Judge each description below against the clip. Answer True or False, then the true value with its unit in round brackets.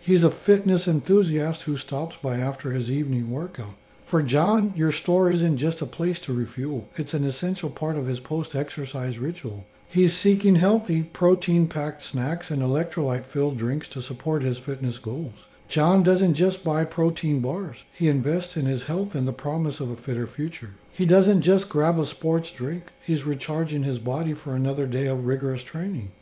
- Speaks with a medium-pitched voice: True (150 Hz)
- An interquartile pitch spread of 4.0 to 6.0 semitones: True (4.4 semitones)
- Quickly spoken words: False (175 wpm)